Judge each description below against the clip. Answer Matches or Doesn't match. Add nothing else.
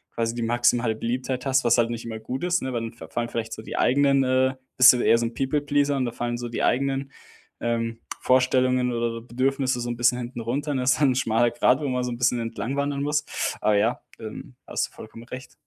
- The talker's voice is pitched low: Matches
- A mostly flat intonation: Matches